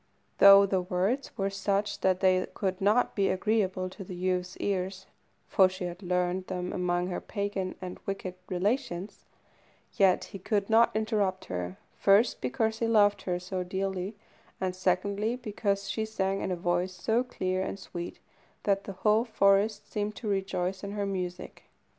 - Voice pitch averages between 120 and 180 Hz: No, high, 195 Hz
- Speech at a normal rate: Yes, average, 165 wpm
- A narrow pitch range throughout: Yes, narrow, 2.0 semitones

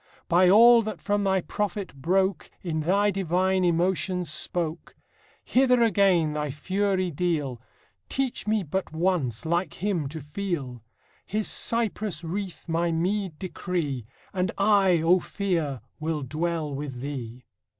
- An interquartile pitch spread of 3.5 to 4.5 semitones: Yes, average, 4.2 semitones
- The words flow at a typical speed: No, slow, 130 wpm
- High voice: No, medium, 180 Hz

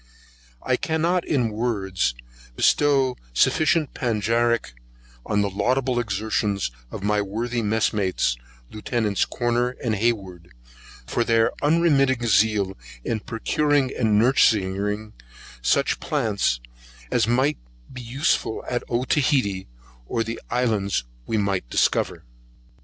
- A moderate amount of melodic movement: Yes, average, 3.6 semitones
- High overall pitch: No, low, 115 Hz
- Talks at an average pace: No, slow, 110 wpm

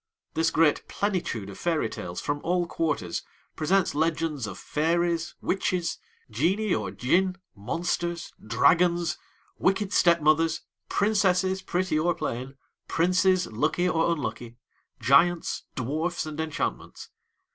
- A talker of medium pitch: Yes, medium, 165 Hz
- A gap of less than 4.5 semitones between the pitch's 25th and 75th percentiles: Yes, average, 3.5 semitones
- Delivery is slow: Yes, slow, 115 wpm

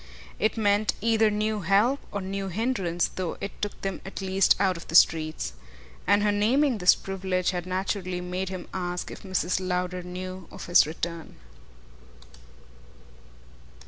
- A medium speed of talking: Yes, average, 150 wpm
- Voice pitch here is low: No, high, 190 Hz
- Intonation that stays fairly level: Yes, narrow, 2.3 semitones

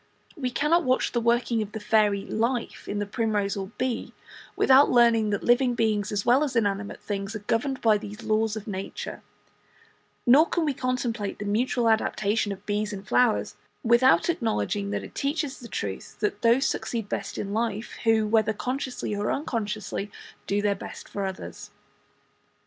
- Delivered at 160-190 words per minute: Yes, average, 175 wpm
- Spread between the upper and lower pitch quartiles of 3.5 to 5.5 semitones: No, average, 3.1 semitones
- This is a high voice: Yes, high, 220 Hz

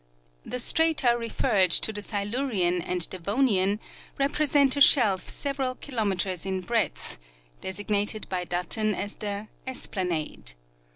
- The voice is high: Yes, high, 205 Hz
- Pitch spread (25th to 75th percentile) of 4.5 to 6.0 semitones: Yes, average, 5.2 semitones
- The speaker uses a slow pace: Yes, slow, 125 wpm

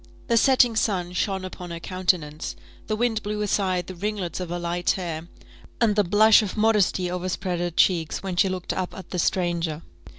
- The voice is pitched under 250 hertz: Yes, medium, 185 Hz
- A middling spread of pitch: Yes, average, 3.1 semitones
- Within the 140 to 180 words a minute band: No, average, 190 wpm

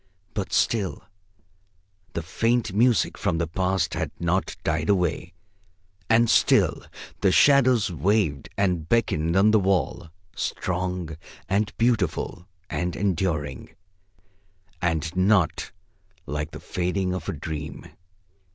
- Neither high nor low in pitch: No, very low, 90 Hz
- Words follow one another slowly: Yes, slow, 115 wpm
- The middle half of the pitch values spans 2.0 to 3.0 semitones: No, average, 4.0 semitones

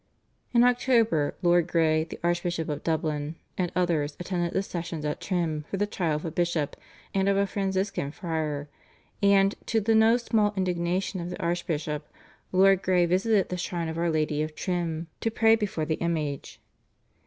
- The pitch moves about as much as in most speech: Yes, average, 3.6 semitones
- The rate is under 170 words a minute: No, average, 175 wpm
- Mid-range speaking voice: Yes, medium, 175 Hz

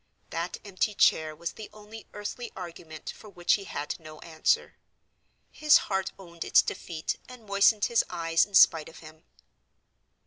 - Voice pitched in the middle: Yes, medium, 180 Hz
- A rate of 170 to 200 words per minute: No, average, 160 wpm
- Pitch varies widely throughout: No, average, 4.2 semitones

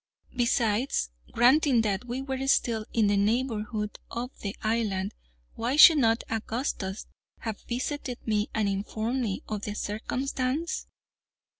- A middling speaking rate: No, slow, 130 wpm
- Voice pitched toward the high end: Yes, high, 230 Hz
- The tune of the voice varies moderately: Yes, average, 3.4 semitones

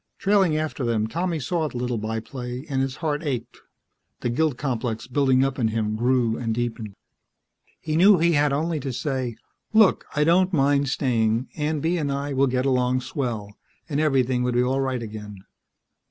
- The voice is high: No, low, 130 Hz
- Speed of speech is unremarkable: Yes, average, 185 wpm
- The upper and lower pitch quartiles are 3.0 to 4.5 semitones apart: Yes, average, 3.7 semitones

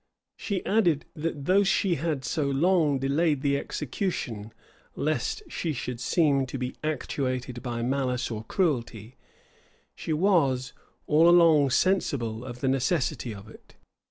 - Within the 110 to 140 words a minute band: Yes, slow, 135 wpm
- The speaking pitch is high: No, medium, 140 Hz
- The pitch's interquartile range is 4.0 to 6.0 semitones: Yes, average, 4.7 semitones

